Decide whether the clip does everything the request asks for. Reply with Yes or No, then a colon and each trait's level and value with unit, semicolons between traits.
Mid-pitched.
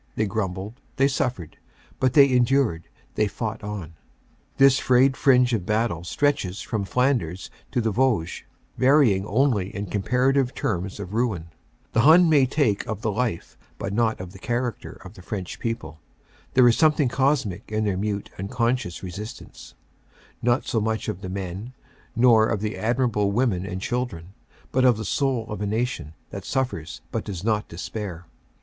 No: low, 110 Hz